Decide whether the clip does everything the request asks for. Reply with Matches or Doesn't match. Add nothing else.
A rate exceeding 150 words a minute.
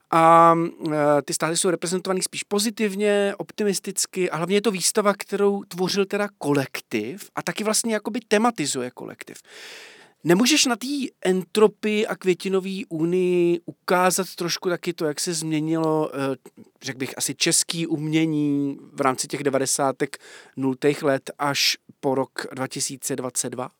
Doesn't match